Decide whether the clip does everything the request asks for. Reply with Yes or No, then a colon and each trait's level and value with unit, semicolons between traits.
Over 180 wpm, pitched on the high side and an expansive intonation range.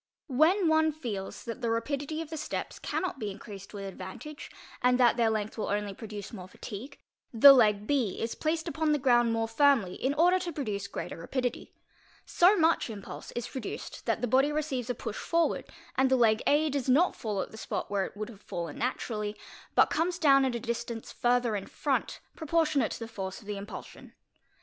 Yes: average, 200 wpm; high, 245 Hz; wide, 5.8 semitones